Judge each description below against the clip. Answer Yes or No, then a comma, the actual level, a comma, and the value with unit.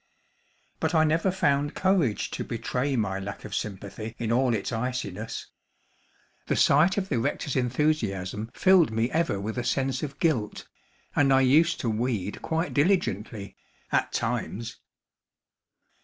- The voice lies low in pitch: Yes, low, 125 Hz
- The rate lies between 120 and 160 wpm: Yes, average, 140 wpm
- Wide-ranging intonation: Yes, wide, 5.9 semitones